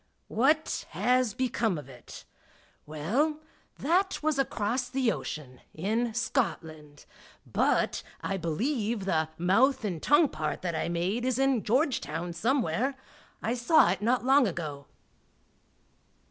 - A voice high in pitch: Yes, high, 225 Hz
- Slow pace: Yes, slow, 125 wpm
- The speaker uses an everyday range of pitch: No, wide, 7.7 semitones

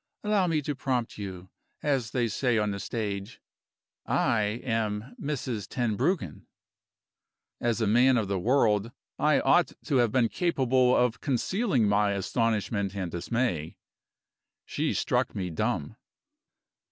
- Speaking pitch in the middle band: No, low, 115 Hz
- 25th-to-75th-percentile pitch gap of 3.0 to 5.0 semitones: Yes, average, 4.2 semitones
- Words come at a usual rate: No, slow, 130 wpm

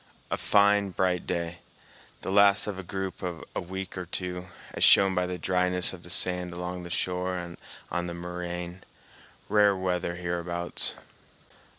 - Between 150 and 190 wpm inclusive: Yes, average, 160 wpm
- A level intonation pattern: Yes, narrow, 1.3 semitones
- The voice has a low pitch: Yes, very low, 90 Hz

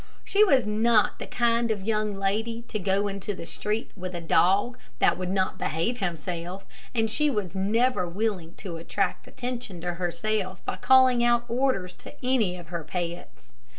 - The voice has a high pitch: Yes, high, 200 Hz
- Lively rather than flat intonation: No, average, 4.6 semitones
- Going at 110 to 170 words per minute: No, average, 180 wpm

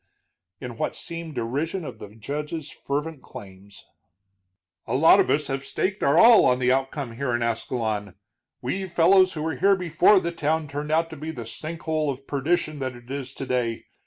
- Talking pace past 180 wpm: Yes, average, 190 wpm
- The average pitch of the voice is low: No, medium, 145 Hz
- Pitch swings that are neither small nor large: Yes, average, 4.5 semitones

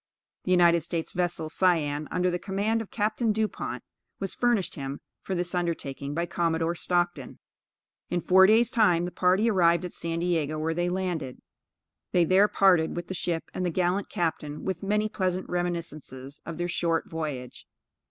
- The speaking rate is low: No, average, 170 wpm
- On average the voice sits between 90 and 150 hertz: No, medium, 175 Hz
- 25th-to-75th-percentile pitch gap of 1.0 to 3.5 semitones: Yes, narrow, 2.4 semitones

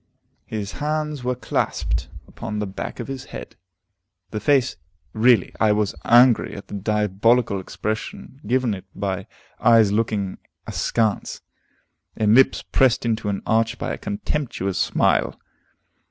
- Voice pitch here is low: Yes, low, 110 Hz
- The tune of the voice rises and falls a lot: No, average, 3.5 semitones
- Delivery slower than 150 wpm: Yes, slow, 135 wpm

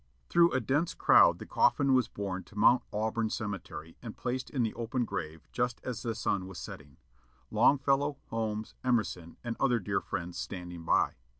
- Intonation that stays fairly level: No, average, 5.2 semitones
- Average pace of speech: Yes, average, 175 wpm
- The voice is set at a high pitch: No, low, 115 Hz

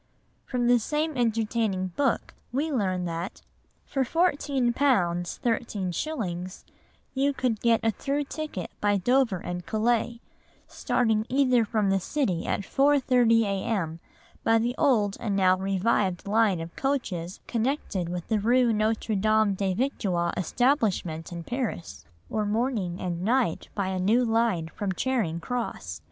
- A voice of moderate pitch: No, high, 220 Hz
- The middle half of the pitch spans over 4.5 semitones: Yes, average, 4.9 semitones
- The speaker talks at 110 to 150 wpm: Yes, average, 140 wpm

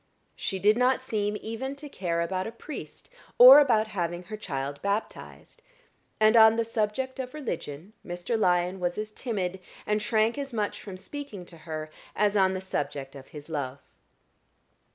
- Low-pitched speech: No, high, 205 Hz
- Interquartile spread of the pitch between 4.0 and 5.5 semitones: Yes, average, 4.6 semitones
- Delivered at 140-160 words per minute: No, average, 170 wpm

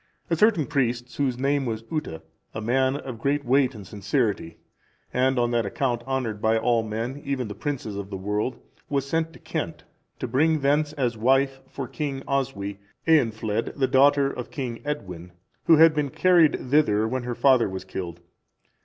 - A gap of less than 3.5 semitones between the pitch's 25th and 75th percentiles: No, average, 4.2 semitones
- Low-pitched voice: Yes, low, 130 Hz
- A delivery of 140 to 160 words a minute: No, average, 180 wpm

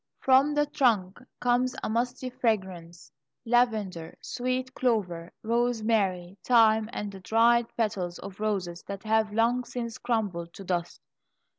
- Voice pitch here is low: No, high, 220 Hz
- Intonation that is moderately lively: Yes, average, 4.4 semitones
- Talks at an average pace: No, slow, 130 wpm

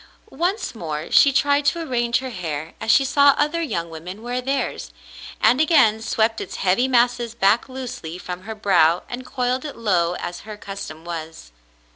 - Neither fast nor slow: Yes, average, 175 wpm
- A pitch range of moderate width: No, wide, 6.7 semitones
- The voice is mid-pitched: No, high, 225 Hz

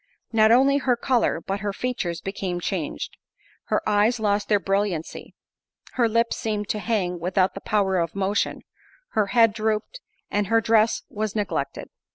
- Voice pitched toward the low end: No, high, 210 Hz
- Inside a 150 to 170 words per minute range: Yes, average, 160 wpm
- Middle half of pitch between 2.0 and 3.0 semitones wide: Yes, average, 2.7 semitones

